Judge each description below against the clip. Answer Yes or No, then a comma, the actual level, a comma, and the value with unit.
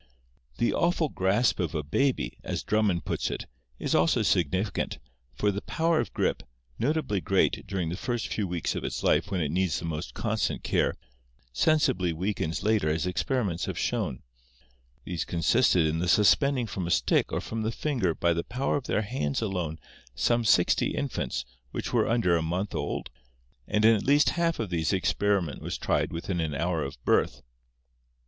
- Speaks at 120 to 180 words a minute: No, average, 190 wpm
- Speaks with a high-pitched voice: No, very low, 95 Hz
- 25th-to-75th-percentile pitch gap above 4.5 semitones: Yes, average, 5.3 semitones